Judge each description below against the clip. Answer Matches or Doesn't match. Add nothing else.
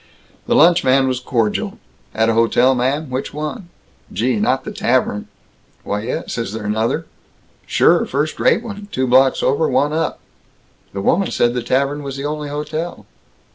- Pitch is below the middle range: Matches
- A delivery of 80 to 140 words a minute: Doesn't match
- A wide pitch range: Doesn't match